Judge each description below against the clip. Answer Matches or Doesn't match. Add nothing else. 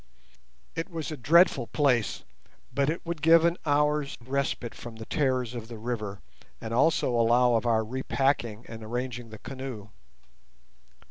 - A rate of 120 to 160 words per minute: Matches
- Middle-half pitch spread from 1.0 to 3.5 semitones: Doesn't match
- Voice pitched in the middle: Doesn't match